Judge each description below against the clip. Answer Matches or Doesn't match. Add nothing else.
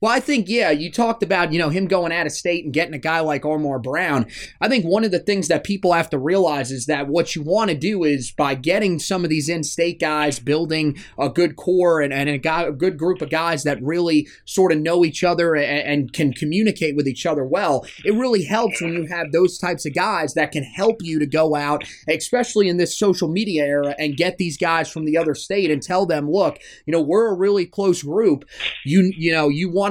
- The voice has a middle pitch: Matches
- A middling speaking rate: Doesn't match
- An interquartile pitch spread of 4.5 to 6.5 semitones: Doesn't match